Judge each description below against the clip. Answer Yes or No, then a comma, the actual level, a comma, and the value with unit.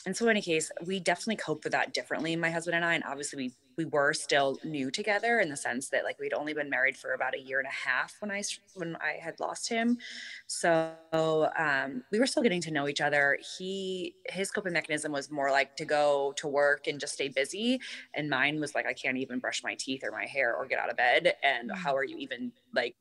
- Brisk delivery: Yes, fast, 250 wpm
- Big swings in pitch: Yes, wide, 5.8 semitones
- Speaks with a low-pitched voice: No, medium, 160 Hz